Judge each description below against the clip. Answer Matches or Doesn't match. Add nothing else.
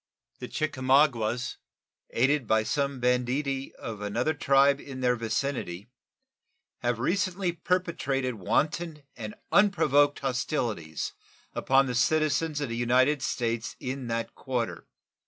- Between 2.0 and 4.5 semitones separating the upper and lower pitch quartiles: Matches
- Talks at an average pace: Doesn't match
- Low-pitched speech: Matches